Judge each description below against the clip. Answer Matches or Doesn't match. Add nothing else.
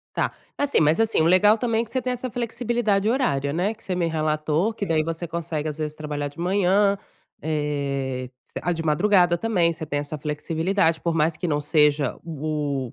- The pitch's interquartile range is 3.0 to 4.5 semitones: Doesn't match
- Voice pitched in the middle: Matches